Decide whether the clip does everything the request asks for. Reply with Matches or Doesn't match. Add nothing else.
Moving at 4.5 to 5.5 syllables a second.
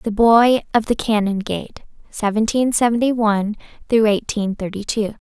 Matches